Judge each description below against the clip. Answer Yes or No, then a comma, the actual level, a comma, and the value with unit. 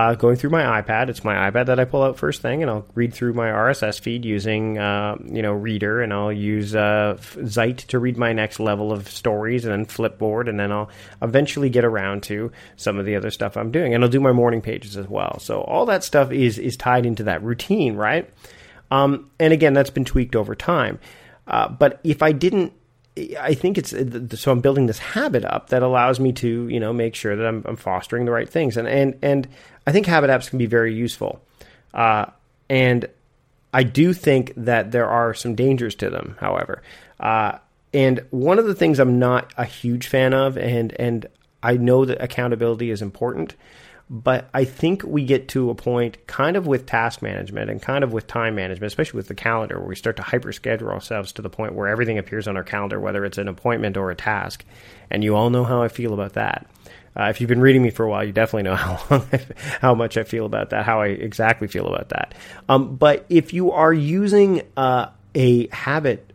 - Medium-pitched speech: No, low, 120 Hz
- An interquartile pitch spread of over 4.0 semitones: No, average, 3.7 semitones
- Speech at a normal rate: No, fast, 225 wpm